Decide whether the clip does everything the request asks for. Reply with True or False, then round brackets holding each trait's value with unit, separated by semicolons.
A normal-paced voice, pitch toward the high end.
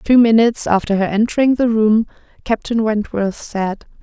True (150 wpm; 220 Hz)